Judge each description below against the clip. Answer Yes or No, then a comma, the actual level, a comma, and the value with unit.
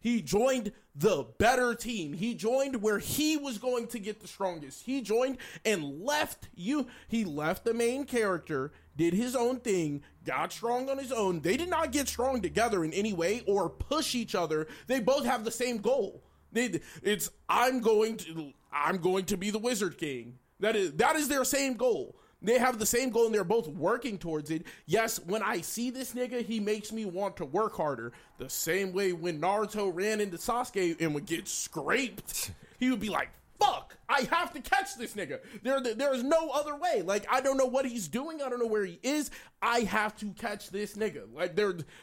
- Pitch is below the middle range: No, high, 225 Hz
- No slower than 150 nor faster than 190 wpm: No, fast, 205 wpm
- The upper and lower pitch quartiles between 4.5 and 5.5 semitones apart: Yes, average, 4.8 semitones